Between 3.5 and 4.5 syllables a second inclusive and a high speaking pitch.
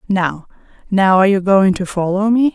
No: 5.1 syllables/s; high, 195 Hz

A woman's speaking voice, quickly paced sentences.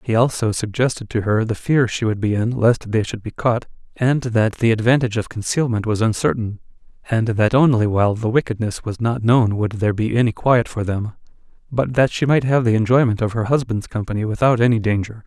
No: male; fast, 210 wpm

